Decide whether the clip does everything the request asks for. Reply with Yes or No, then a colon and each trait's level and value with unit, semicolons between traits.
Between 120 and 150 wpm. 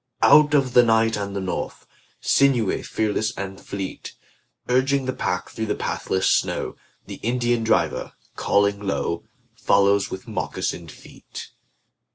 Yes: slow, 135 wpm